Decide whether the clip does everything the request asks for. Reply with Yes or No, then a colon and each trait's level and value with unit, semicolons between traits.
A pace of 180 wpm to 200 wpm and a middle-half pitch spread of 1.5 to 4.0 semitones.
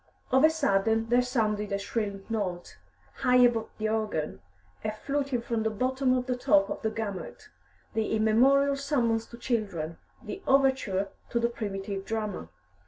No: average, 160 wpm; average, 3.5 semitones